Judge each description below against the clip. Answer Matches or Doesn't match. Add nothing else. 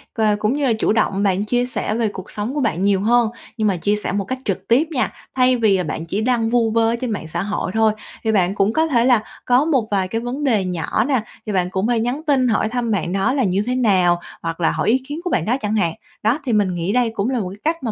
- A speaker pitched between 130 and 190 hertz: Doesn't match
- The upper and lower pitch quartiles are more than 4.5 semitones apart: Doesn't match